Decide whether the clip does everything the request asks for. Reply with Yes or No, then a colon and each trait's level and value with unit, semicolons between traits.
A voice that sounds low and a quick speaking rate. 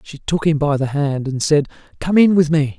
No: medium, 150 Hz; fast, 260 wpm